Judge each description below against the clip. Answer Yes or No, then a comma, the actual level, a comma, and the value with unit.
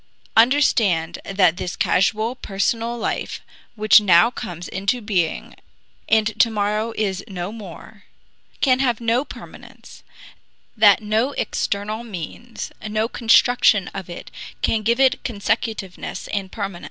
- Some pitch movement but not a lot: Yes, average, 3.1 semitones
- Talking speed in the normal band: No, slow, 125 wpm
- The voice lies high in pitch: Yes, high, 215 Hz